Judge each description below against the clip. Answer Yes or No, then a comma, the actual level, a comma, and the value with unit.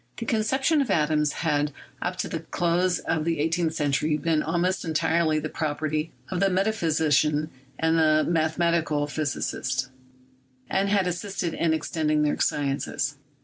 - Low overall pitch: No, medium, 160 Hz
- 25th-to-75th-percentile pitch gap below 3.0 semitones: Yes, narrow, 2.5 semitones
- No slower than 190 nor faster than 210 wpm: No, average, 145 wpm